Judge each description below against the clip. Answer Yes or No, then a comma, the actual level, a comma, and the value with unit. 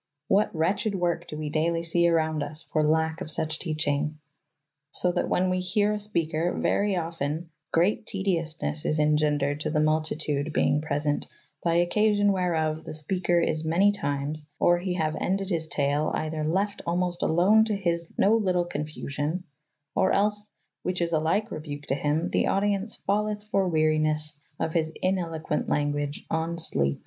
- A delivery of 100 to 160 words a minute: No, average, 170 wpm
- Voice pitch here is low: No, medium, 165 Hz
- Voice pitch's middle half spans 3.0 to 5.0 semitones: Yes, average, 3.3 semitones